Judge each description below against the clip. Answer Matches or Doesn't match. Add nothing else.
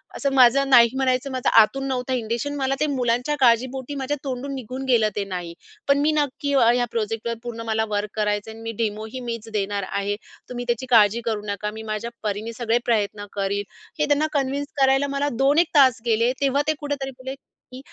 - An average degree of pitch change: Matches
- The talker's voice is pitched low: Doesn't match